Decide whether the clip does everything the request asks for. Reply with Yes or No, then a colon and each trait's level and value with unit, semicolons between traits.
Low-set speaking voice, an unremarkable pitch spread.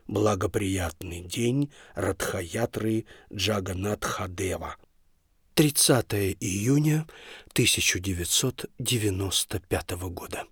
Yes: low, 100 Hz; average, 3.9 semitones